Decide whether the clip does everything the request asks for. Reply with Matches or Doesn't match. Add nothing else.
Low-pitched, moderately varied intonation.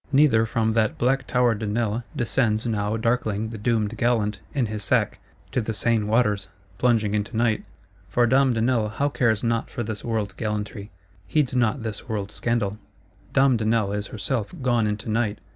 Doesn't match